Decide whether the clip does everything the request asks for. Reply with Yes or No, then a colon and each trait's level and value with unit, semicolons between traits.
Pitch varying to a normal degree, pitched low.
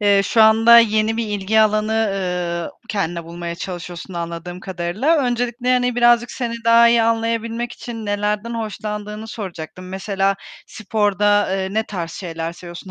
No: average, 3.9 semitones; high, 210 Hz